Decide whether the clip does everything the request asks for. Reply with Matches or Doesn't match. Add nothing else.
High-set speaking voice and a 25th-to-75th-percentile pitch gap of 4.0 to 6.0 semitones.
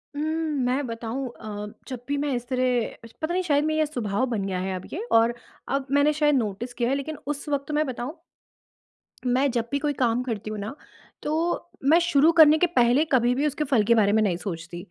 Matches